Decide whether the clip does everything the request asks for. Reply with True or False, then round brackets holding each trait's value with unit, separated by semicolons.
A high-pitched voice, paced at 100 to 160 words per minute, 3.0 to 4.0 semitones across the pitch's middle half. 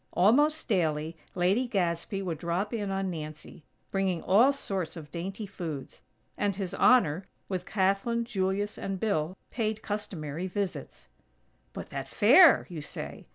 True (195 Hz; 140 wpm; 3.7 semitones)